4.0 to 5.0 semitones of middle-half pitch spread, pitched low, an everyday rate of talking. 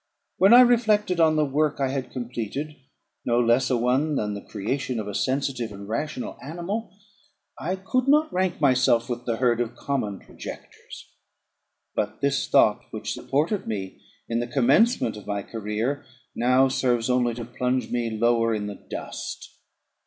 Yes: average, 4.7 semitones; low, 125 Hz; average, 165 wpm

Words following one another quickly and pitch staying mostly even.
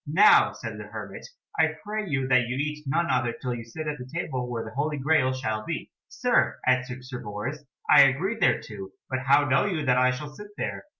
No: fast, 220 wpm; average, 3.4 semitones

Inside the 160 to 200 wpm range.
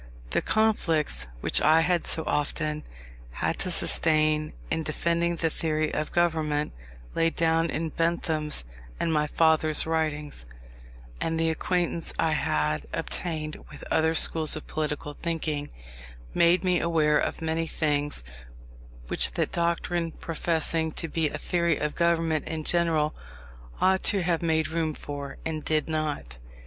No: average, 140 wpm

